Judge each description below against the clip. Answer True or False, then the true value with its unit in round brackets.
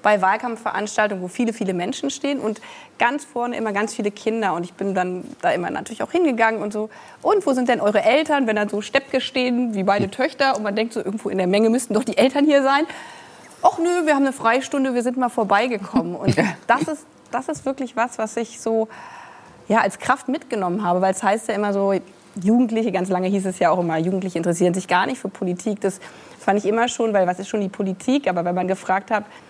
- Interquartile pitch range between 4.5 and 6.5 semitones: True (5.0 semitones)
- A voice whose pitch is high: True (220 Hz)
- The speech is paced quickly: True (235 wpm)